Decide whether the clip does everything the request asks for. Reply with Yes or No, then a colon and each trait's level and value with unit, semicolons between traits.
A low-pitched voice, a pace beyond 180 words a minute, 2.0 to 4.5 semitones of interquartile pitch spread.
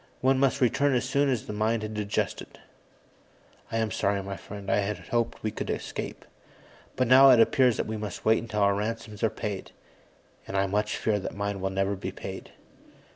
Yes: low, 110 Hz; average, 200 wpm; average, 2.8 semitones